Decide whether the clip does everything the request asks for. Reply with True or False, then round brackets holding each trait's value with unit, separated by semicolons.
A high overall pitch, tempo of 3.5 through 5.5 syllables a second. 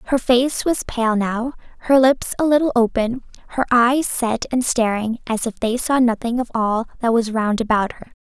True (240 Hz; 4.5 syllables/s)